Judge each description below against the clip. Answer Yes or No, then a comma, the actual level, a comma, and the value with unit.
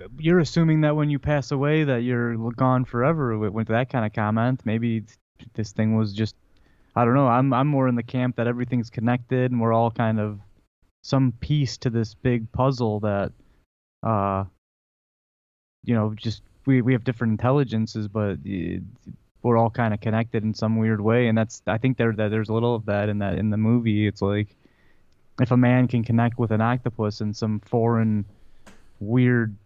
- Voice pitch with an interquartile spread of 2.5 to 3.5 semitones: Yes, average, 2.9 semitones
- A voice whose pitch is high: No, low, 115 Hz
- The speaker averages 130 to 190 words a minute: Yes, average, 185 wpm